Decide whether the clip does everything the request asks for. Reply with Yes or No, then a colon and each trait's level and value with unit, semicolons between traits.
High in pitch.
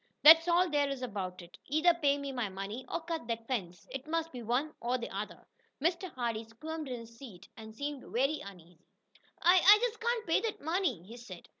Yes: very high, 260 Hz